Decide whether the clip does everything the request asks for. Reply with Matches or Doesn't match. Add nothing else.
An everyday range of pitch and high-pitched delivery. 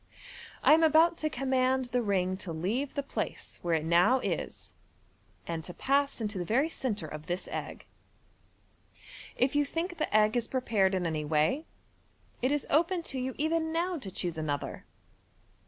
Doesn't match